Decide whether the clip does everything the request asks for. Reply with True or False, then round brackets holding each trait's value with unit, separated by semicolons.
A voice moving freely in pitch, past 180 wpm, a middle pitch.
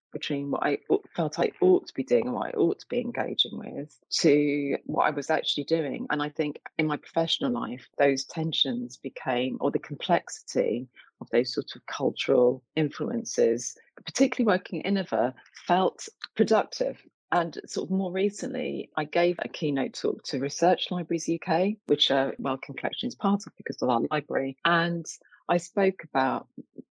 False (6.0 semitones; 170 wpm; 165 Hz)